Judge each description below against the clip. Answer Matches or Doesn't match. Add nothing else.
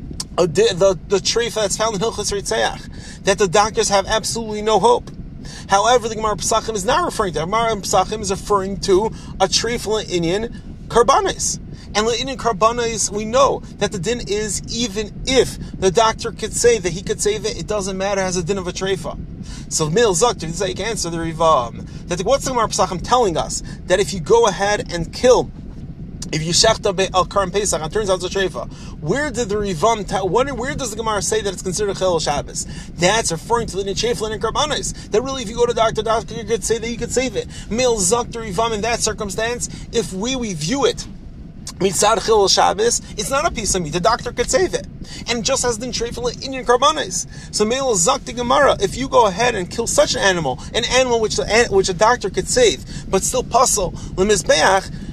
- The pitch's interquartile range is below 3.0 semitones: Doesn't match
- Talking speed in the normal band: Doesn't match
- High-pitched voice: Matches